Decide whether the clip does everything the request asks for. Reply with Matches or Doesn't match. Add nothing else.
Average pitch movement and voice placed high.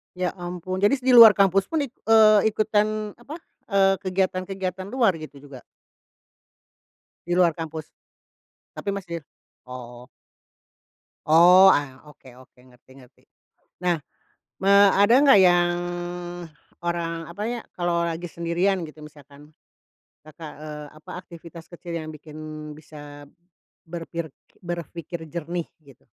Doesn't match